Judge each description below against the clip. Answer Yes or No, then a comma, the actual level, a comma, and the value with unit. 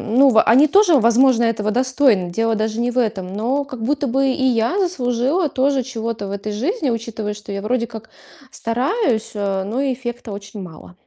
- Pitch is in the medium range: No, high, 235 Hz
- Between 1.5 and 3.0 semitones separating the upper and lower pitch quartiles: No, average, 3.7 semitones